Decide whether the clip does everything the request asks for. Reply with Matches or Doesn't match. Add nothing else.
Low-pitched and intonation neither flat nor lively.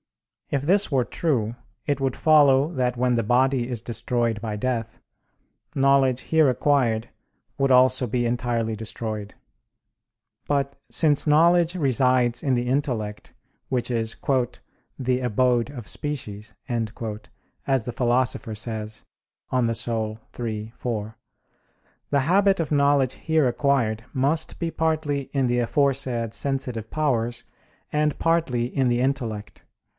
Matches